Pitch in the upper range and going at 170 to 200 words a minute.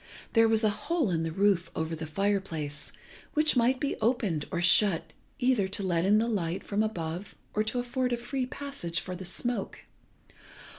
Yes: high, 205 Hz; average, 190 wpm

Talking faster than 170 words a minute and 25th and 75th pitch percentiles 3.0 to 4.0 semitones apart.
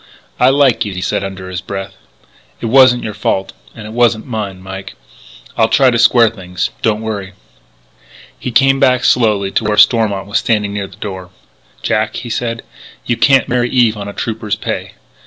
Yes: average, 185 wpm; average, 3.4 semitones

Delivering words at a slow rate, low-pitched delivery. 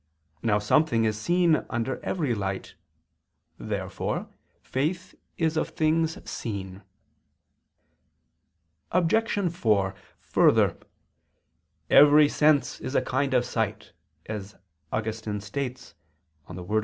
Yes: slow, 100 wpm; low, 125 Hz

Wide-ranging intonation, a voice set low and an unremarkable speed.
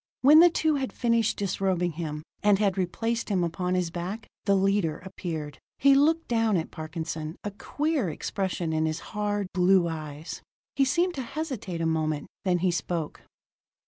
No: wide, 5.7 semitones; high, 190 Hz; average, 170 wpm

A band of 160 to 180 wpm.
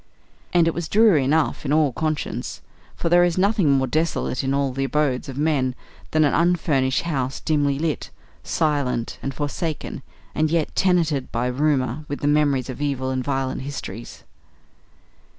Yes: average, 165 wpm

